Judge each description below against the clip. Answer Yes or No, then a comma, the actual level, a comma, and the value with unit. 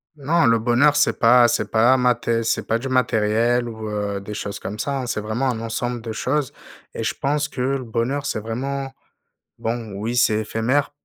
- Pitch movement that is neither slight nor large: Yes, average, 3.0 semitones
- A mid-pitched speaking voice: No, low, 120 Hz